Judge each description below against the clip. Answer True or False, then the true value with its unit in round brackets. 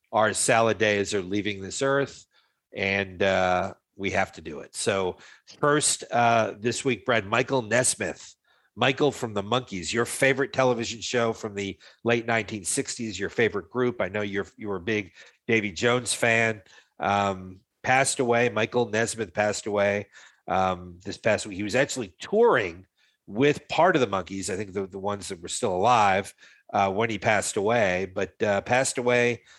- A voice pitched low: True (110 Hz)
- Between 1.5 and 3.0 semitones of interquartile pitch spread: False (3.7 semitones)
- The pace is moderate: True (170 wpm)